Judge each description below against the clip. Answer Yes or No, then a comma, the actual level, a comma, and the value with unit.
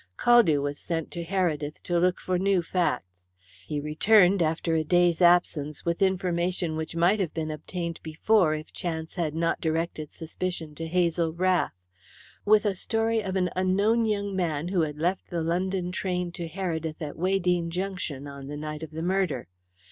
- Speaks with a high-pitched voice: No, medium, 170 Hz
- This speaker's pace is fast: No, average, 175 wpm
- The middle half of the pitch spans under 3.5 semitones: Yes, average, 2.8 semitones